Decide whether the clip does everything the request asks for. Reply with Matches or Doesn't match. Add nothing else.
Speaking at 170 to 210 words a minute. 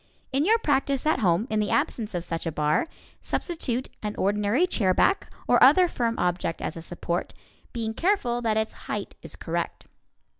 Matches